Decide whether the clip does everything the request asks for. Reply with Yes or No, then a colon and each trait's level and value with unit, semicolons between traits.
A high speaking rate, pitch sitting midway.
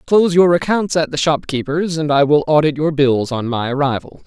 Yes: fast, 210 wpm; medium, 150 Hz